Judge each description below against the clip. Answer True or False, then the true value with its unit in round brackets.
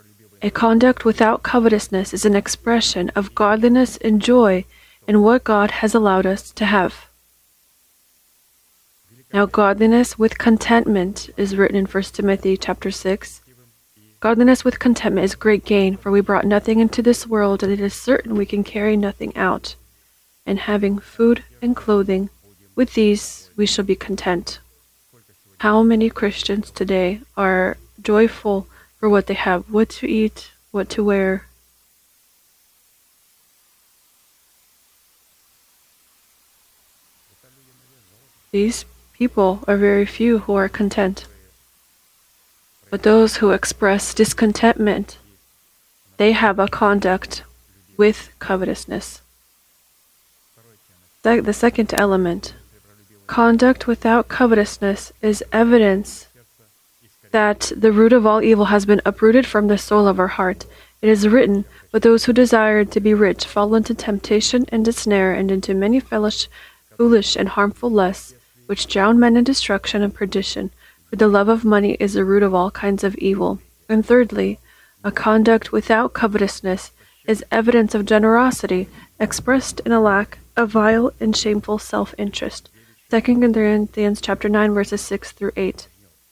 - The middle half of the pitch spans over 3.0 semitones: False (2.6 semitones)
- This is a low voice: False (205 Hz)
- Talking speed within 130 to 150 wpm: True (135 wpm)